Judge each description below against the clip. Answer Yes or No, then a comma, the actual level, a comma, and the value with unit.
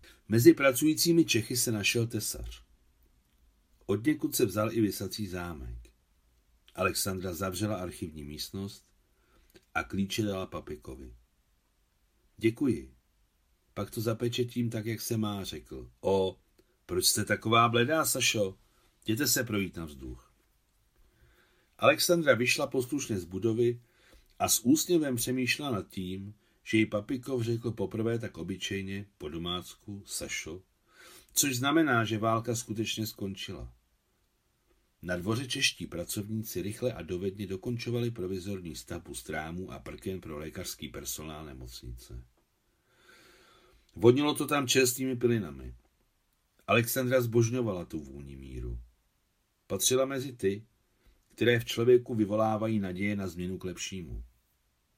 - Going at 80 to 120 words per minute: Yes, slow, 115 wpm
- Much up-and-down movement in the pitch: Yes, wide, 5.7 semitones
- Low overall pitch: Yes, low, 105 Hz